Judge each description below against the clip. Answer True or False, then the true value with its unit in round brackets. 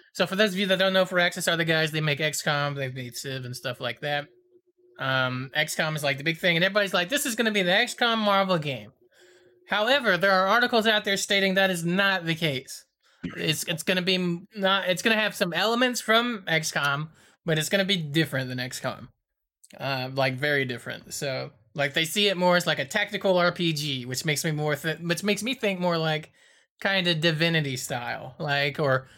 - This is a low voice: False (170 Hz)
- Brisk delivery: True (225 wpm)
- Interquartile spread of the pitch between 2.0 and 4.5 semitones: False (5.4 semitones)